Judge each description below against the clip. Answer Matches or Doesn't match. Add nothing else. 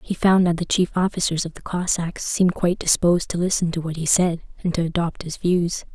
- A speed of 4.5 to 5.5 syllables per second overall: Doesn't match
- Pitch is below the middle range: Doesn't match